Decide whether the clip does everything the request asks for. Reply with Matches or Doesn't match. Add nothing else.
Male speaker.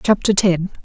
Doesn't match